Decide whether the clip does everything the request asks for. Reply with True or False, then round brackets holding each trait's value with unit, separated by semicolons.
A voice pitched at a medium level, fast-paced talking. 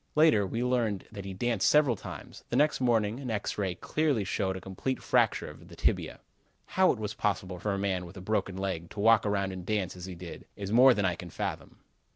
False (100 Hz; 230 wpm)